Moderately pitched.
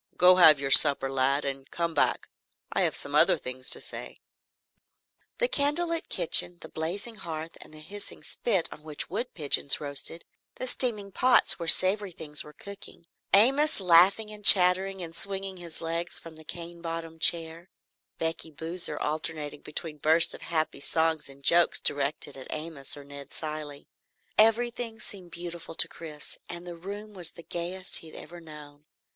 Yes: medium, 170 Hz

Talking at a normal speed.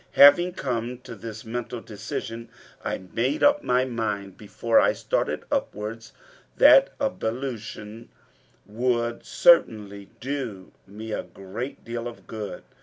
No: slow, 120 wpm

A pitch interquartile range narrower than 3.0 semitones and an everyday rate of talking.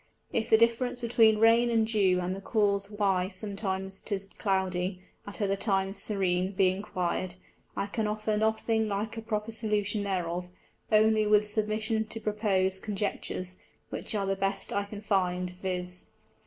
Yes: narrow, 2.4 semitones; average, 155 wpm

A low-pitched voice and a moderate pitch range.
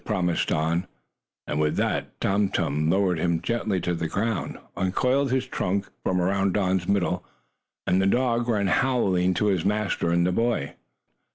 Yes: very low, 95 Hz; average, 3.3 semitones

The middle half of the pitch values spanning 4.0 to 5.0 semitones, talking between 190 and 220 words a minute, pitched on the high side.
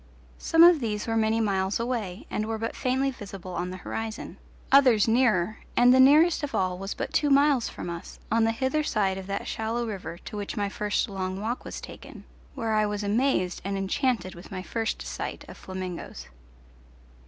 Yes: average, 4.4 semitones; average, 195 wpm; high, 220 Hz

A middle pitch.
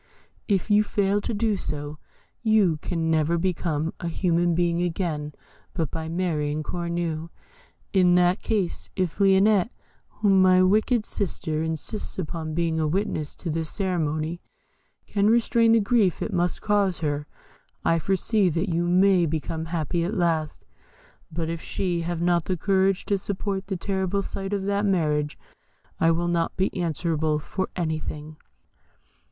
Yes: medium, 175 Hz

